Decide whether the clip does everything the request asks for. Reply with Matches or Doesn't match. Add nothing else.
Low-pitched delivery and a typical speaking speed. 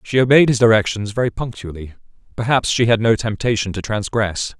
Matches